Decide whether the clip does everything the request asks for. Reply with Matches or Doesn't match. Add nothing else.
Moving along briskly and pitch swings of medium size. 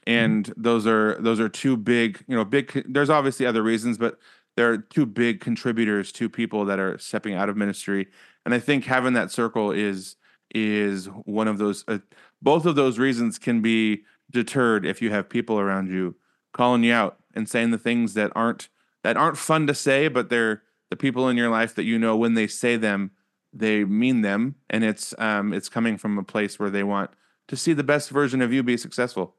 Matches